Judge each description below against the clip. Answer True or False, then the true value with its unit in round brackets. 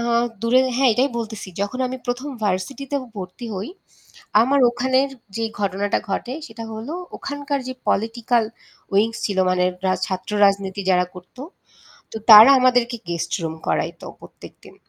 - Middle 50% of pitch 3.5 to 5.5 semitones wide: True (4.6 semitones)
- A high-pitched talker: True (225 Hz)